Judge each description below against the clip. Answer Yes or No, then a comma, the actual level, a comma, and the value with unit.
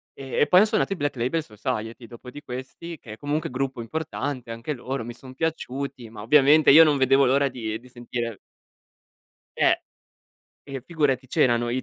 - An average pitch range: Yes, average, 3.4 semitones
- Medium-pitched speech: No, low, 130 Hz